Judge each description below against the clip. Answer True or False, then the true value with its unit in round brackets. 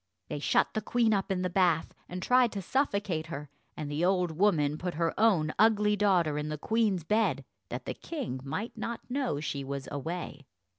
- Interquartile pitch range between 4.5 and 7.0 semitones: True (5.6 semitones)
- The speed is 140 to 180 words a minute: False (195 wpm)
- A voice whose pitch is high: False (180 Hz)